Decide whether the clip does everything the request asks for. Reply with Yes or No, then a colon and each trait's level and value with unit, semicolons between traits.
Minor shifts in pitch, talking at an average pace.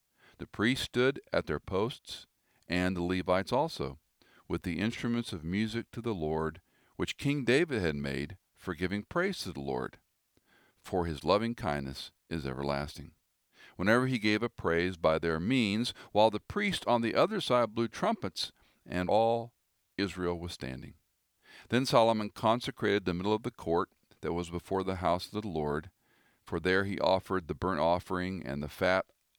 No: average, 5.2 semitones; average, 170 wpm